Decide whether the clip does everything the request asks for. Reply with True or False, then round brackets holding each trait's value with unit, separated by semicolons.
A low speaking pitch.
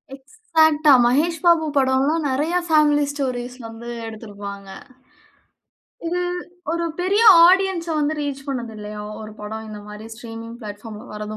False (265 Hz)